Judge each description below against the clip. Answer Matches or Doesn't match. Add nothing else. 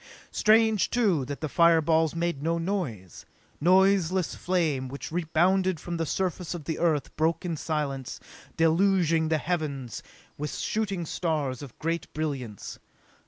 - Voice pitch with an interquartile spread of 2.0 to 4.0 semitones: Matches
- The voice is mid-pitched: Matches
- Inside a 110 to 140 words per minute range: Matches